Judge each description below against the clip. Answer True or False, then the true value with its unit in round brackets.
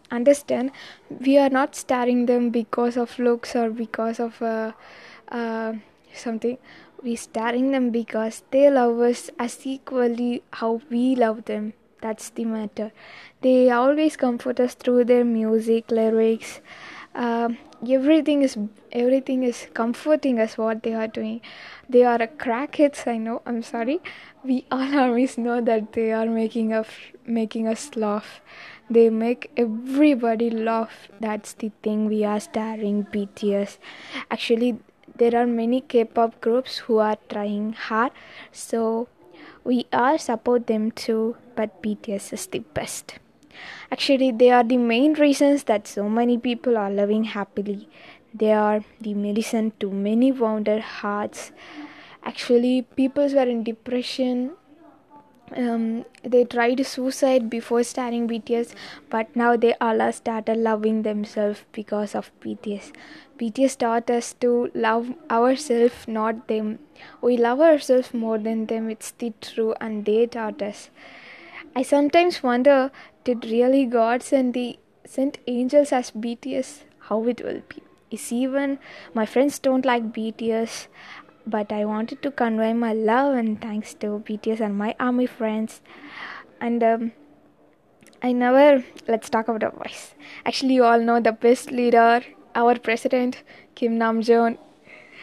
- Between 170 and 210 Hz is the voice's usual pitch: False (235 Hz)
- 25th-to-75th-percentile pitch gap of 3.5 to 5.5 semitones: False (2.5 semitones)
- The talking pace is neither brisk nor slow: False (140 wpm)